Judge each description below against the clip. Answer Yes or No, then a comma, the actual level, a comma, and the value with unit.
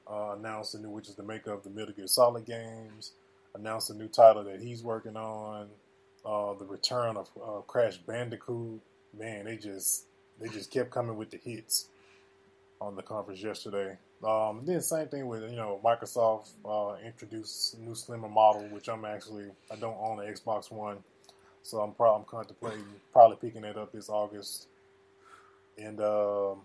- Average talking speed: Yes, average, 180 wpm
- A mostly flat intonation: Yes, narrow, 1.8 semitones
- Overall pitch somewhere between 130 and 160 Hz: No, low, 105 Hz